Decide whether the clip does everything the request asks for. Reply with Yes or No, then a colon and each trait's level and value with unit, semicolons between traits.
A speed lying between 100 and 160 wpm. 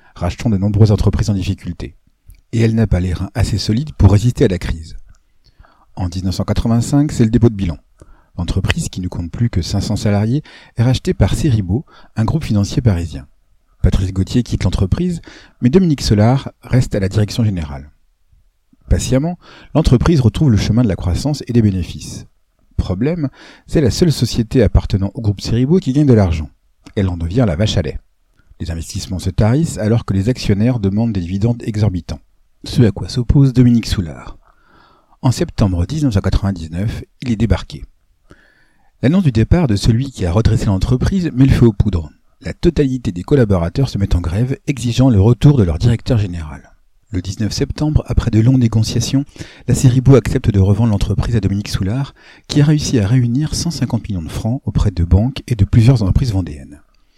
No: average, 180 wpm